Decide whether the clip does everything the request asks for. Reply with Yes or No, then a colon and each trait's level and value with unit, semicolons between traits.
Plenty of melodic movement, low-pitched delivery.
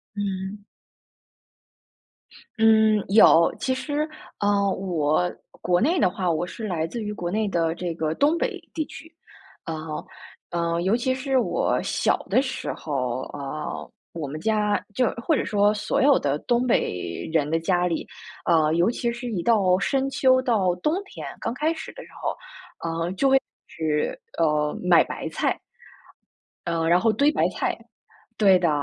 No: wide, 6.6 semitones; high, 195 Hz